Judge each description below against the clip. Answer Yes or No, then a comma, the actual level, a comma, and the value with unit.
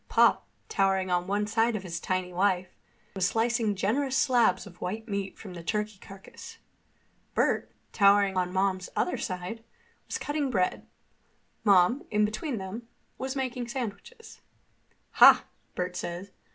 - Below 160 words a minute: Yes, average, 140 wpm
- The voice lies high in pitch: Yes, high, 200 Hz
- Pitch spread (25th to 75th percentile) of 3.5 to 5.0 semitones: Yes, average, 3.8 semitones